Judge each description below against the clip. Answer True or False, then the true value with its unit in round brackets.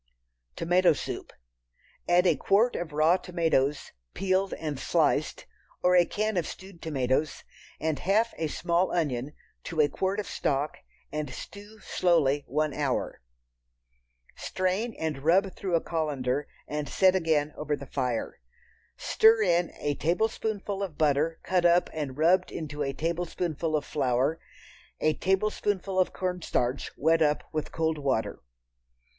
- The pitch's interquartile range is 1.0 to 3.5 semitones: False (4.0 semitones)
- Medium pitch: True (165 Hz)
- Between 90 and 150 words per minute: True (140 wpm)